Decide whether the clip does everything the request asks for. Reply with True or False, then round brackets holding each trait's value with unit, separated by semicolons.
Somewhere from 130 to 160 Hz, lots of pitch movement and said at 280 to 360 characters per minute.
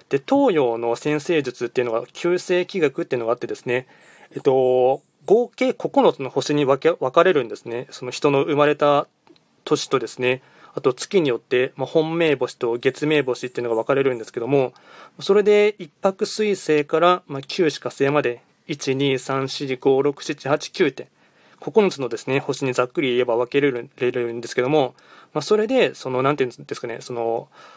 False (140 Hz; 4.5 semitones; 335 characters per minute)